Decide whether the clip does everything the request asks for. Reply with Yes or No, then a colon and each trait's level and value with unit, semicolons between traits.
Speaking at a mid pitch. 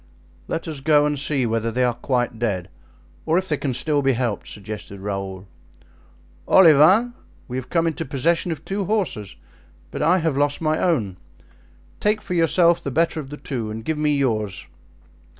Yes: medium, 145 Hz